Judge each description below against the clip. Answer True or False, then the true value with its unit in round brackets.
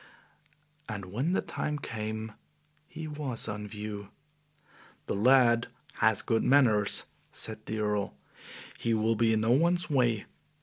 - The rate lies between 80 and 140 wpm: True (135 wpm)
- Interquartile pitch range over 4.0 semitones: False (3.4 semitones)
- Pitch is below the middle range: True (110 Hz)